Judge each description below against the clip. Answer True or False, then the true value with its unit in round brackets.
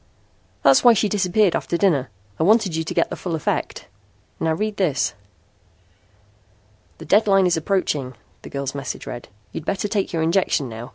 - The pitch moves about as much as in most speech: False (5.7 semitones)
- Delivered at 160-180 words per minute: True (170 wpm)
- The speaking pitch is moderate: True (170 Hz)